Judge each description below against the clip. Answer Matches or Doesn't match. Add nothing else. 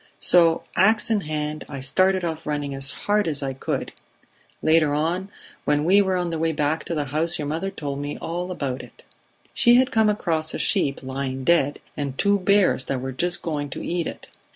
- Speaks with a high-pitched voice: Doesn't match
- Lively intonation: Doesn't match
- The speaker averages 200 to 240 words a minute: Matches